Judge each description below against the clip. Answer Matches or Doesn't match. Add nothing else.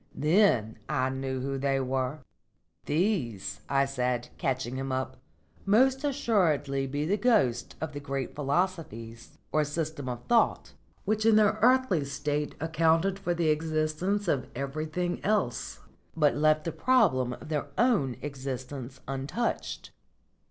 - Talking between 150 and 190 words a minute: Doesn't match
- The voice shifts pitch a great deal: Matches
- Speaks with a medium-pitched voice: Matches